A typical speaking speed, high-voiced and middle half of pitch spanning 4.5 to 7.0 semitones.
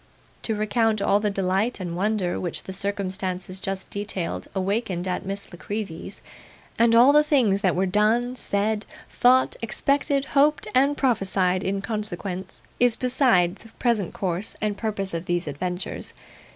No: average, 150 wpm; high, 200 Hz; average, 3.6 semitones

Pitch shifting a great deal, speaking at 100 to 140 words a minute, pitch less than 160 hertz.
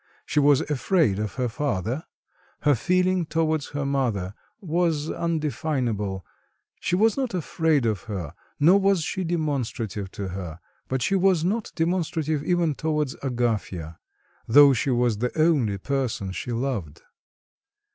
Yes: wide, 6.6 semitones; slow, 135 wpm; medium, 140 Hz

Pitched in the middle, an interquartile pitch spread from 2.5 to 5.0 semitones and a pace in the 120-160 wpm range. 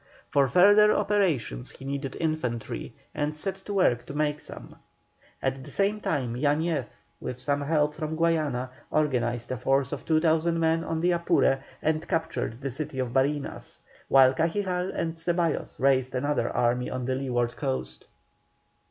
Yes: medium, 145 Hz; average, 4.1 semitones; average, 155 wpm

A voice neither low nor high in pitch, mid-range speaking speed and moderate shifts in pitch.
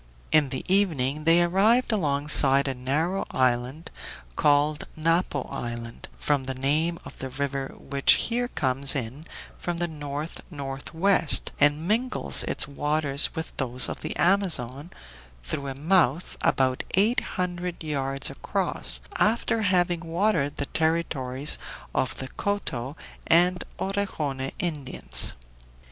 No: medium, 150 Hz; slow, 125 wpm; average, 4.5 semitones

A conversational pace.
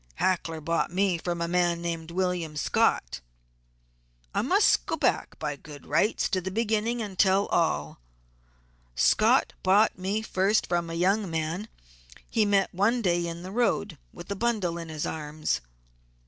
Yes: average, 160 wpm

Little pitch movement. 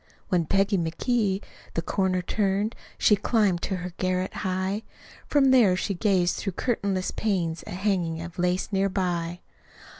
Yes: narrow, 2.3 semitones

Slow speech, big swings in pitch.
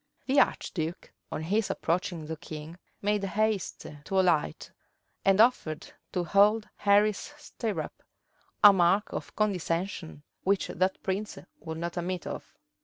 No: slow, 130 wpm; average, 3.7 semitones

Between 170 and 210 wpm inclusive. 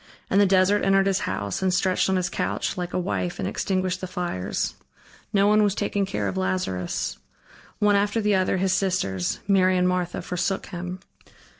Yes: average, 185 wpm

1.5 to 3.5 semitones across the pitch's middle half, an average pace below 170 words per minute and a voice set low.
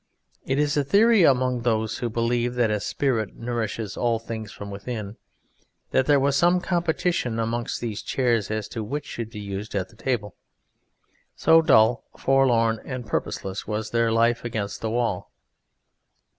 Yes: average, 3.2 semitones; average, 155 wpm; low, 115 Hz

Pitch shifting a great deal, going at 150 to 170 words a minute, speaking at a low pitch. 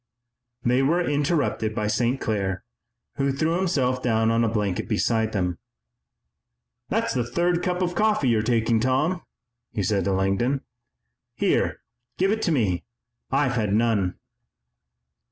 No: wide, 6.4 semitones; average, 140 wpm; low, 120 Hz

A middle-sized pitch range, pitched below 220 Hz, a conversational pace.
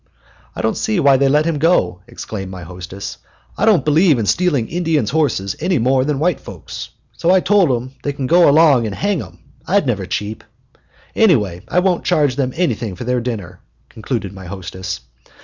No: wide, 8.0 semitones; low, 135 Hz; average, 190 wpm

